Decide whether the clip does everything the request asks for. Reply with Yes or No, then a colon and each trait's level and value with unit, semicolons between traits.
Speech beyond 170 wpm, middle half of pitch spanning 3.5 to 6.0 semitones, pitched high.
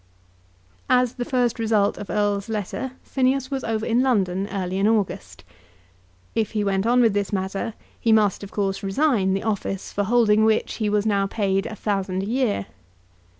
No: average, 180 wpm; average, 2.7 semitones; high, 210 Hz